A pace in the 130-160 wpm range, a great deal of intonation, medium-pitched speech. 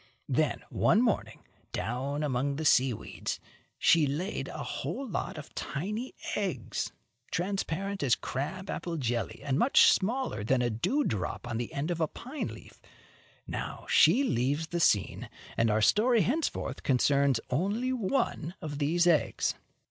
Yes: average, 150 wpm; wide, 7.5 semitones; medium, 155 Hz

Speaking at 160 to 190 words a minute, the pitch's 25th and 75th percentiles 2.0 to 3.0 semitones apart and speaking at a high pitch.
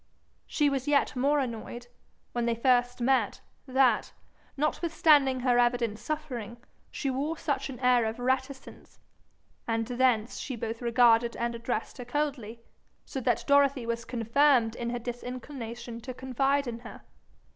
No: average, 145 wpm; narrow, 2.5 semitones; high, 245 Hz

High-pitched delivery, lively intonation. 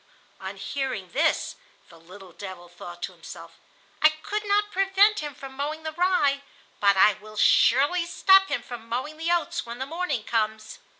Yes: very high, 275 Hz; wide, 8.1 semitones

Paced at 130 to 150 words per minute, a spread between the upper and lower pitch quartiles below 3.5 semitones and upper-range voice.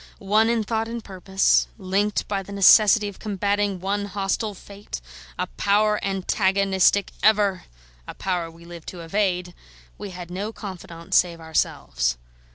Yes: average, 145 wpm; narrow, 2.4 semitones; high, 195 Hz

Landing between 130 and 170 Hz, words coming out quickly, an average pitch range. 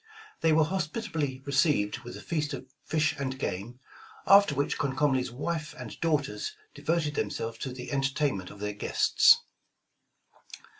No: medium, 140 Hz; average, 145 wpm; average, 3.5 semitones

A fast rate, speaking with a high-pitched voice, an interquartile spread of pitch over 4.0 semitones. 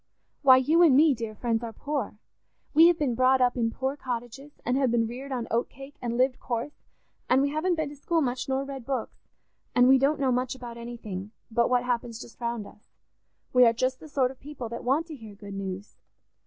No: fast, 225 wpm; very high, 255 Hz; average, 2.8 semitones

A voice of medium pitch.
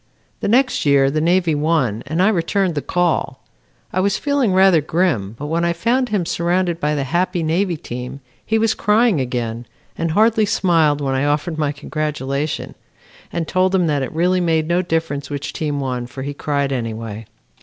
Yes: medium, 160 Hz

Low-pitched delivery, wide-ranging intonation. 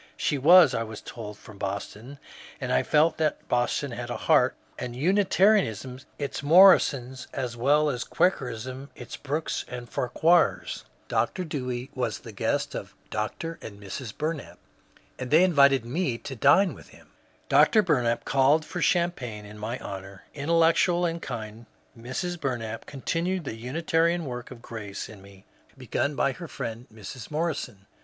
Yes: low, 130 Hz; wide, 5.9 semitones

